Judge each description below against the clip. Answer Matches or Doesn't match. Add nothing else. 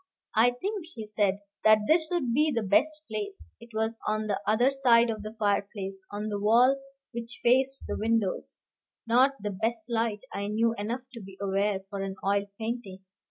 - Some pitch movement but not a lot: Matches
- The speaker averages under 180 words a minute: Doesn't match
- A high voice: Matches